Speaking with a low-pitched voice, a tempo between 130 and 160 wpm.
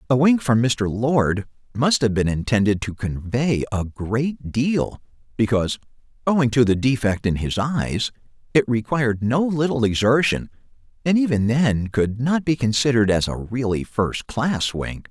Yes: low, 120 Hz; average, 155 wpm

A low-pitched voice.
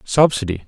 Yes: low, 120 Hz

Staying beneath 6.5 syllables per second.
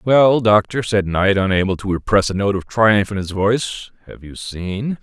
Yes: 4.6 syllables/s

